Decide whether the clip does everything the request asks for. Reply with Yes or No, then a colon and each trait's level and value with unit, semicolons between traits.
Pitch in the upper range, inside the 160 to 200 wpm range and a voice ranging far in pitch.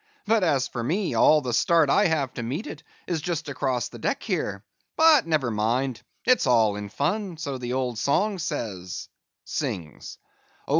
No: medium, 140 Hz; average, 170 wpm; wide, 6.0 semitones